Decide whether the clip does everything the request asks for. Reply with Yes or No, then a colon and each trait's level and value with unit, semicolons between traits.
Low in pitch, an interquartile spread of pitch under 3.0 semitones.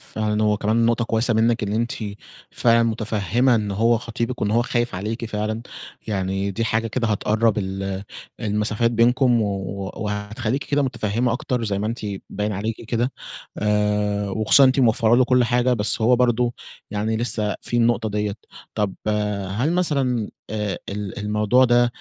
Yes: low, 110 Hz; narrow, 2.4 semitones